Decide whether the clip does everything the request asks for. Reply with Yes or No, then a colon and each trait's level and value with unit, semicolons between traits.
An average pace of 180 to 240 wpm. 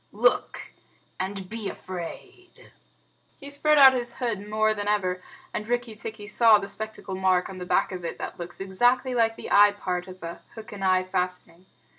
Yes: average, 185 wpm